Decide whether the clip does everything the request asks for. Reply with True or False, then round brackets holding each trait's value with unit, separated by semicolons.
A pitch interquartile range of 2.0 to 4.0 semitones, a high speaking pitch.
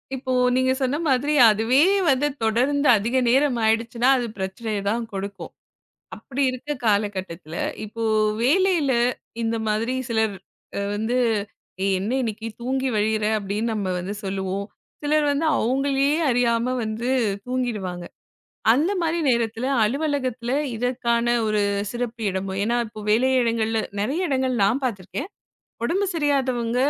True (3.6 semitones; 235 Hz)